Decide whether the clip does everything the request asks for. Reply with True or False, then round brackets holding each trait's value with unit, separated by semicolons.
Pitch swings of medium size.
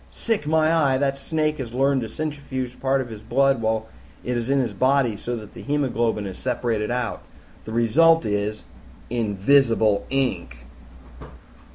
True (3.9 semitones)